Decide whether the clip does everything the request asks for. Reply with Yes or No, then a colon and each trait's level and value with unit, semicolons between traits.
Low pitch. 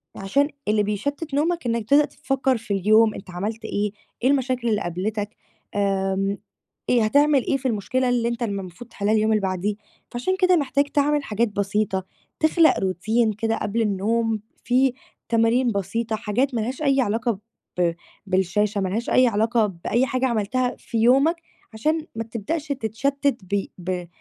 No: high, 225 Hz